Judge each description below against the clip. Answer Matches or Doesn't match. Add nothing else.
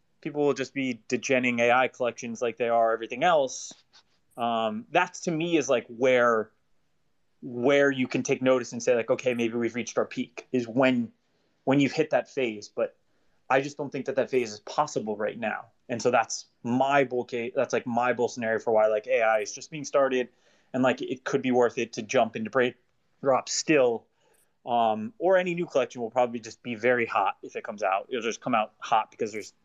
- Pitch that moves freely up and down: Doesn't match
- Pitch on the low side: Matches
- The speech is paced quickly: Matches